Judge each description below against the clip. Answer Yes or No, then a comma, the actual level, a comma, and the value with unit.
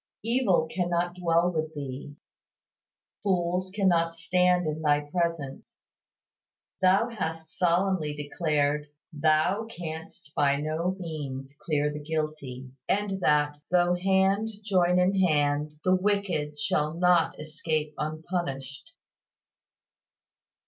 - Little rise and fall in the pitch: No, average, 3.5 semitones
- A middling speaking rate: No, slow, 105 wpm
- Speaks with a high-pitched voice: No, medium, 165 Hz